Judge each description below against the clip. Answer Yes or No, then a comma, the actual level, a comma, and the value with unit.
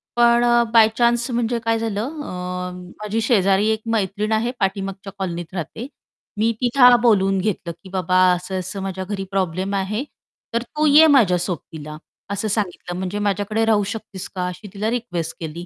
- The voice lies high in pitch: Yes, high, 200 Hz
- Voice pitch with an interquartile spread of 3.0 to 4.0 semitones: Yes, average, 3.5 semitones